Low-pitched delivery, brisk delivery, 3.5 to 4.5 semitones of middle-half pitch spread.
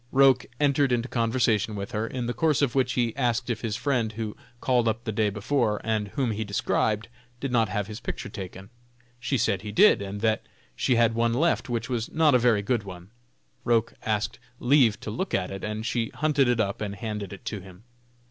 No: low, 115 Hz; fast, 215 wpm; average, 3.0 semitones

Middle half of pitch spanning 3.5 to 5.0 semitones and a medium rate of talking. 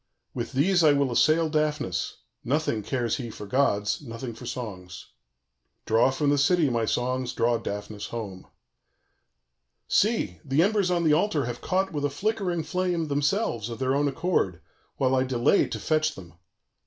No: wide, 5.4 semitones; average, 165 wpm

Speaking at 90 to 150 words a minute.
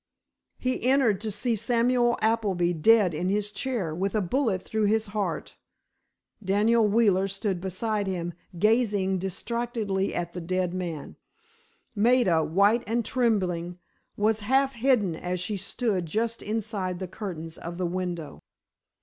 Yes: average, 140 wpm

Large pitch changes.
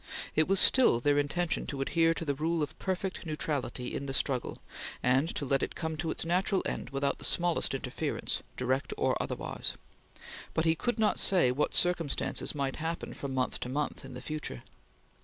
No: average, 3.7 semitones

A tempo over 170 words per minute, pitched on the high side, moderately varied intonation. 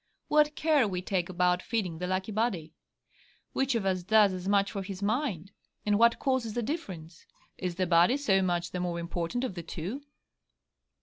Yes: average, 185 wpm; high, 195 Hz; average, 4.6 semitones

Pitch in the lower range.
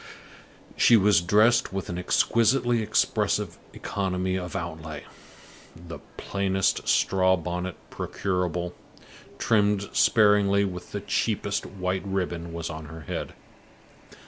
Yes: very low, 95 Hz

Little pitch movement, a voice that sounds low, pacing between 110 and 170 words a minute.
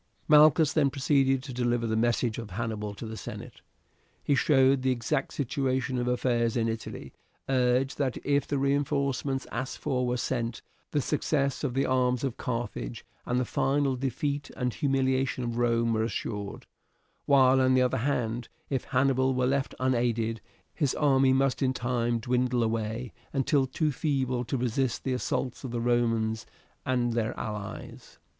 Yes: narrow, 2.3 semitones; low, 125 Hz; average, 165 wpm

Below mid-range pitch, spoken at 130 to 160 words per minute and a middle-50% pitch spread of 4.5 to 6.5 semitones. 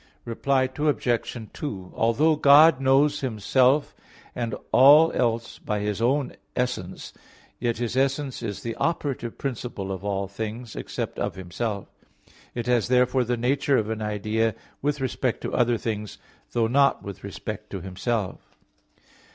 No: low, 120 Hz; average, 145 wpm; average, 3.9 semitones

